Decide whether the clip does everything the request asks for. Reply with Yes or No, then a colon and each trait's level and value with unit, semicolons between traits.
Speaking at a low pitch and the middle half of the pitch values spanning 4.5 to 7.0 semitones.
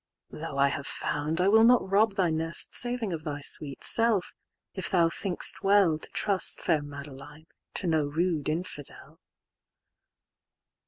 No: medium, 165 Hz; average, 4.9 semitones